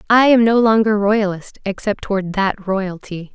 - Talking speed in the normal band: Yes, average, 160 wpm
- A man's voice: No, female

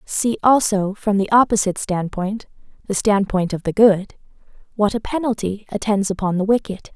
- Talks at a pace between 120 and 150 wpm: Yes, average, 140 wpm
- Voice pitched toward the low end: No, high, 205 Hz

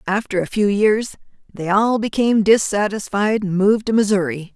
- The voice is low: No, high, 205 Hz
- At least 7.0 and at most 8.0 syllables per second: No, 5.2 syllables/s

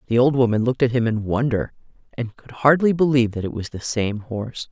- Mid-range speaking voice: No, low, 120 Hz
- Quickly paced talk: Yes, fast, 230 wpm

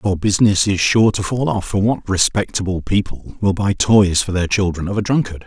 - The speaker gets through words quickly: Yes, fast, 220 wpm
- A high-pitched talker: No, low, 100 Hz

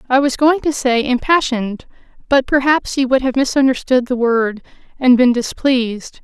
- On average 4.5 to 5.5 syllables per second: Yes, 4.9 syllables/s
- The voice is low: No, very high, 260 Hz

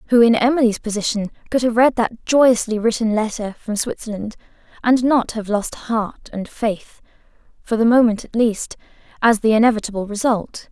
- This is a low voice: No, high, 225 Hz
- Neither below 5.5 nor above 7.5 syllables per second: No, 4.9 syllables/s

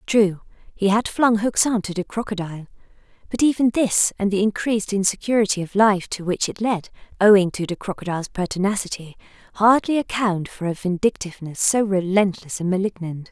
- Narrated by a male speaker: No, female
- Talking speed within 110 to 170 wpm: Yes, average, 160 wpm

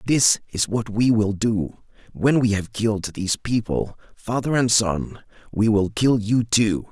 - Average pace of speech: Yes, average, 175 wpm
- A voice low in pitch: Yes, low, 110 Hz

